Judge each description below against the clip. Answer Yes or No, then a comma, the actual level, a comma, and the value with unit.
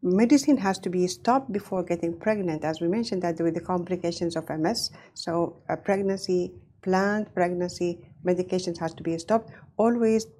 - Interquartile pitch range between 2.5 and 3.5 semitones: Yes, average, 3.1 semitones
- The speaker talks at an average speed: Yes, average, 160 wpm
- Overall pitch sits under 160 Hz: No, medium, 180 Hz